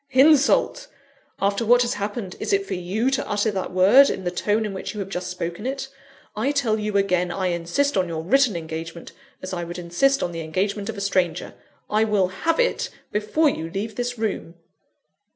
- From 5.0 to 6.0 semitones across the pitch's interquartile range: Yes, average, 5.3 semitones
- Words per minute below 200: No, fast, 205 wpm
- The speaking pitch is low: No, high, 205 Hz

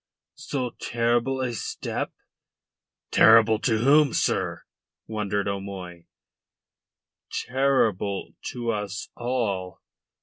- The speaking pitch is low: Yes, low, 110 Hz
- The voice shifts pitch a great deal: No, average, 3.8 semitones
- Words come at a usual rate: No, slow, 80 wpm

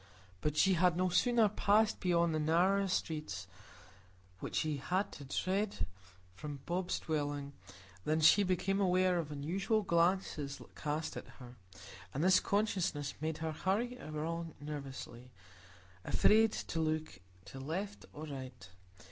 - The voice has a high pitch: No, medium, 165 Hz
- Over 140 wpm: No, slow, 135 wpm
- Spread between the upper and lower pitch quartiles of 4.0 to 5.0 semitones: Yes, average, 4.4 semitones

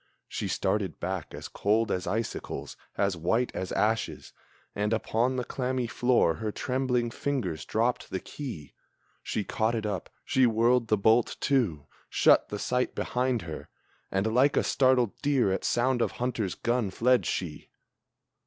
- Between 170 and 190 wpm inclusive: No, average, 155 wpm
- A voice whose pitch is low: Yes, low, 115 Hz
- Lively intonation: No, average, 4.2 semitones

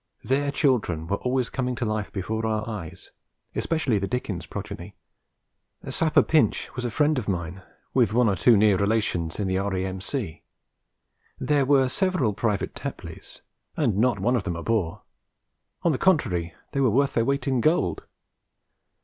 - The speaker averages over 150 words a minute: Yes, average, 165 wpm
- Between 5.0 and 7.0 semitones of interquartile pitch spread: Yes, wide, 5.6 semitones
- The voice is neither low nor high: No, low, 110 Hz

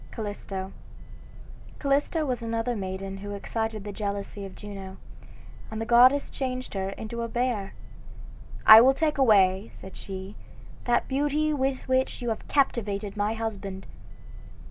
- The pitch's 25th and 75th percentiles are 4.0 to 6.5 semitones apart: Yes, average, 4.3 semitones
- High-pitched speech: Yes, high, 220 Hz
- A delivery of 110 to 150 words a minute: Yes, average, 140 wpm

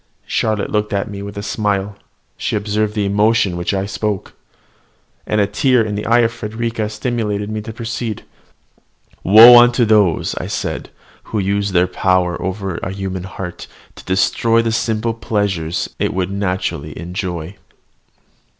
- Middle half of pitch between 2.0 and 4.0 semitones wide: Yes, narrow, 2.6 semitones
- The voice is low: Yes, low, 105 Hz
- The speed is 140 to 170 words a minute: Yes, average, 160 wpm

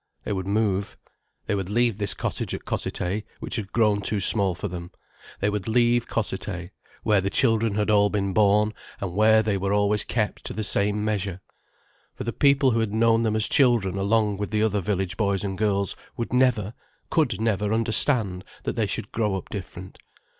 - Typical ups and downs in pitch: No, narrow, 2.3 semitones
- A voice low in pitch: Yes, low, 105 Hz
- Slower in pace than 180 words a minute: No, average, 195 wpm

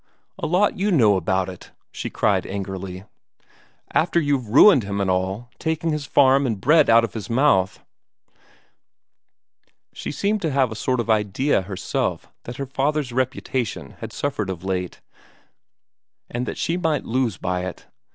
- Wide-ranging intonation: Yes, wide, 6.9 semitones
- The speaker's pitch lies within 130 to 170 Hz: No, low, 120 Hz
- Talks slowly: No, average, 160 wpm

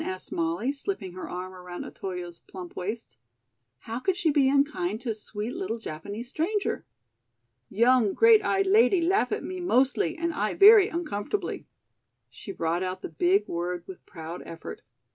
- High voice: Yes, high, 220 Hz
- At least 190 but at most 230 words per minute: No, average, 160 wpm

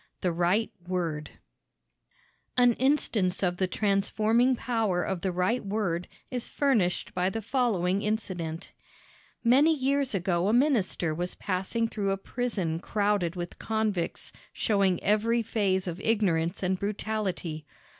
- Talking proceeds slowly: Yes, slow, 130 wpm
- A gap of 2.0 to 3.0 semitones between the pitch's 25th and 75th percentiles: No, average, 4.1 semitones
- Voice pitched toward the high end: Yes, high, 200 Hz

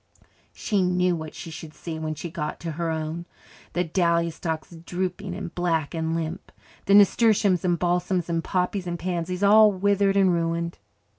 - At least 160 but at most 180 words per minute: Yes, average, 170 wpm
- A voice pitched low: No, medium, 175 Hz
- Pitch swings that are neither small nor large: No, narrow, 2.1 semitones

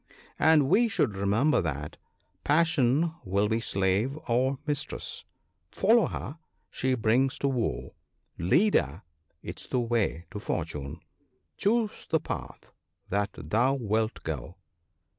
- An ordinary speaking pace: No, slow, 125 wpm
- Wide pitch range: Yes, wide, 7.1 semitones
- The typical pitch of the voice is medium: No, low, 120 Hz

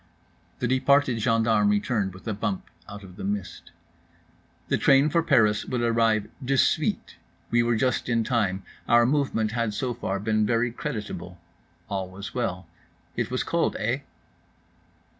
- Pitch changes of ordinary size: Yes, average, 3.2 semitones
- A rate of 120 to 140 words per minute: No, average, 155 wpm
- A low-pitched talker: Yes, low, 115 Hz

